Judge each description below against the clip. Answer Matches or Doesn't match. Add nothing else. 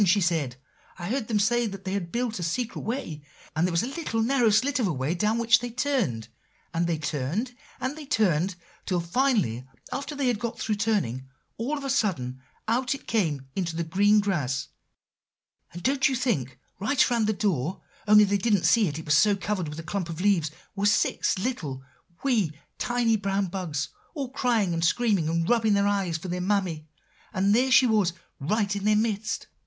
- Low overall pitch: Doesn't match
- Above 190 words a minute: Matches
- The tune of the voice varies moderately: Doesn't match